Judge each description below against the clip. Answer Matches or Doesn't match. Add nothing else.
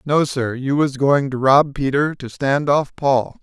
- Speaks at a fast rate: Matches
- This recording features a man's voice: Matches